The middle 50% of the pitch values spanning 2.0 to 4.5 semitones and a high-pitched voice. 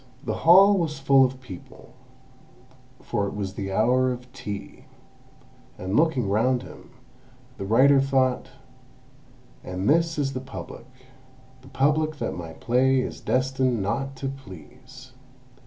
No: average, 3.6 semitones; low, 130 Hz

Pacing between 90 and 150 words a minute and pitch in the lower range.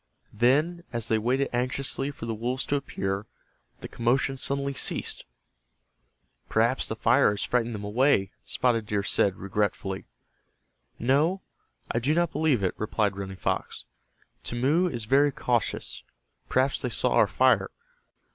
Yes: average, 140 wpm; low, 120 Hz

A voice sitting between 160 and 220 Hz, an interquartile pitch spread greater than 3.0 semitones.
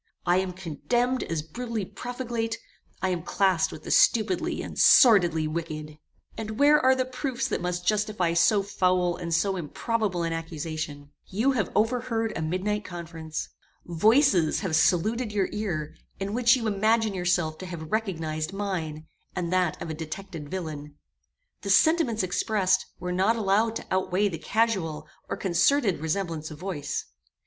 Yes: medium, 185 Hz; average, 5.0 semitones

